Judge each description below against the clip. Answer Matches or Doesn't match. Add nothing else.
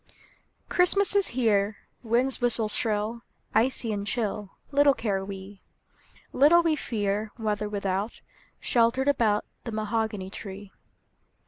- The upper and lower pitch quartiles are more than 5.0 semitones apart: Doesn't match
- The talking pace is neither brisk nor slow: Doesn't match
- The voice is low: Doesn't match